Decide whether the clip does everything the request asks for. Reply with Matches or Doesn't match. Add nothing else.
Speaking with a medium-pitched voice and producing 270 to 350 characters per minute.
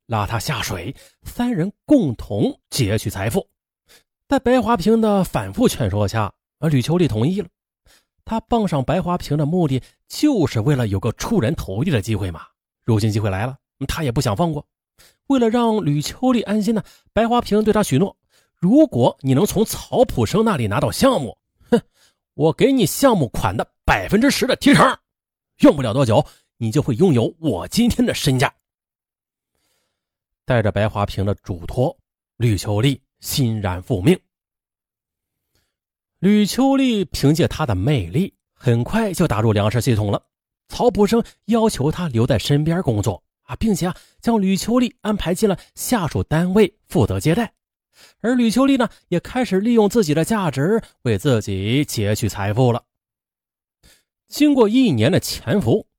Doesn't match